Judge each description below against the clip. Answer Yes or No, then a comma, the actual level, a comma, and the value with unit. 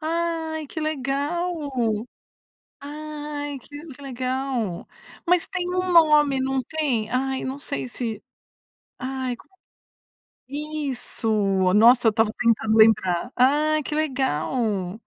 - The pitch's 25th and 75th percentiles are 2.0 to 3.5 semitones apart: No, average, 4.2 semitones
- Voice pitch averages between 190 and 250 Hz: No, very high, 270 Hz